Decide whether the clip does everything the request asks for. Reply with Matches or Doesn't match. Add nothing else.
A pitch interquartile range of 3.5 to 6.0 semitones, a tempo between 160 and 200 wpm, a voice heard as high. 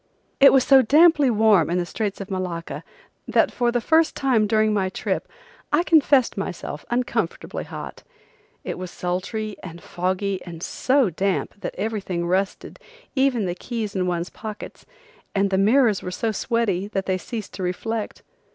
Matches